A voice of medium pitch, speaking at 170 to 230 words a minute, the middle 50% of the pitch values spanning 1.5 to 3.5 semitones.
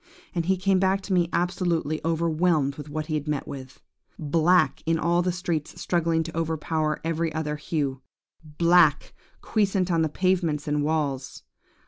No: medium, 165 Hz; average, 160 wpm; narrow, 2.6 semitones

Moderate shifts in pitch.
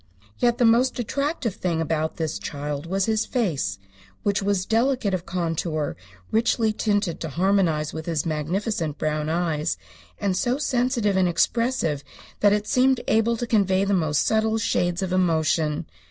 No: wide, 5.8 semitones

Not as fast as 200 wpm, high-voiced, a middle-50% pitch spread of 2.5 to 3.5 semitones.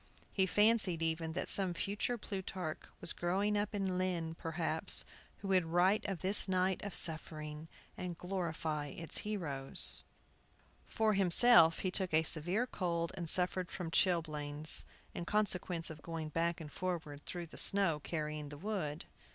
No: average, 150 wpm; medium, 175 Hz; average, 3.0 semitones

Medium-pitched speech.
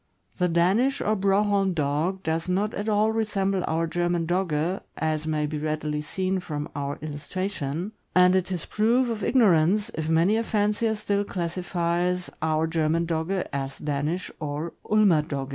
Yes: medium, 175 Hz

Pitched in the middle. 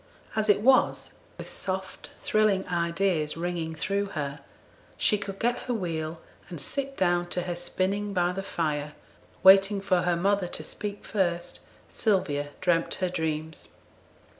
Yes: medium, 180 Hz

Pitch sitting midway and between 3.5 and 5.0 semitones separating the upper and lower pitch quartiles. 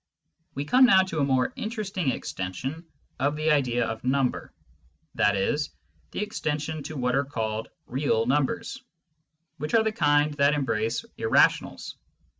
Yes: medium, 145 Hz; average, 4.2 semitones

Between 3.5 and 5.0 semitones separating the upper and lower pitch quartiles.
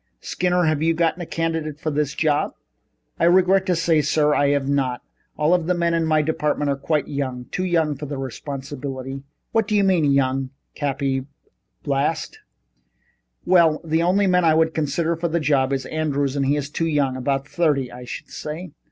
No: average, 3.1 semitones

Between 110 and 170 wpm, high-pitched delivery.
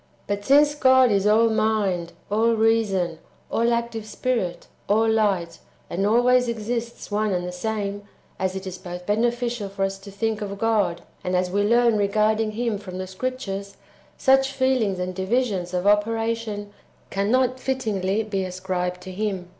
Yes: average, 160 wpm; high, 210 Hz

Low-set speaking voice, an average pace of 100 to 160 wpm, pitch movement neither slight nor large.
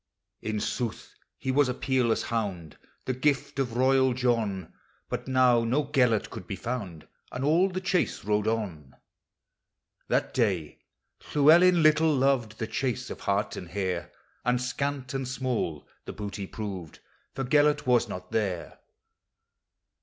Yes: low, 125 Hz; average, 145 wpm; average, 4.6 semitones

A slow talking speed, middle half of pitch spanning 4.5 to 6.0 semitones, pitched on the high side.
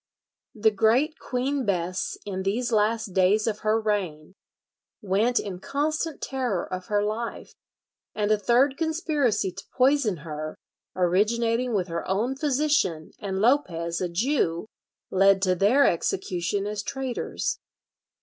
Yes: slow, 130 wpm; average, 5.1 semitones; high, 210 Hz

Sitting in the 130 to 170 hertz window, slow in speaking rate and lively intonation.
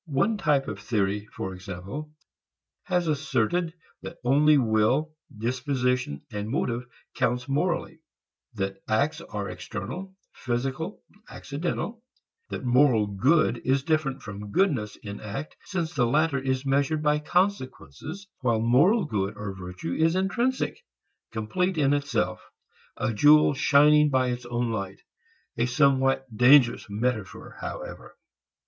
Yes: low, 135 Hz; slow, 125 wpm; wide, 5.8 semitones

